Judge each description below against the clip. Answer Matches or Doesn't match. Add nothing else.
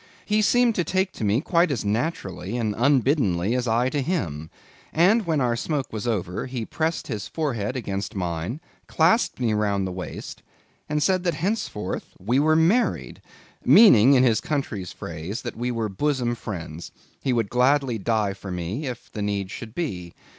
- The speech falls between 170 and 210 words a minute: Matches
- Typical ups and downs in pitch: Doesn't match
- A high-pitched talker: Doesn't match